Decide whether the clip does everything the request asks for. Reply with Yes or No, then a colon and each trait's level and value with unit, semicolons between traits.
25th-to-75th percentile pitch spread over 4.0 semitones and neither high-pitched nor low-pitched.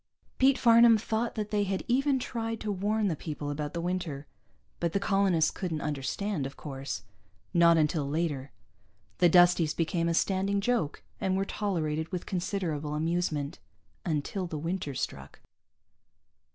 Yes: average, 4.8 semitones; medium, 175 Hz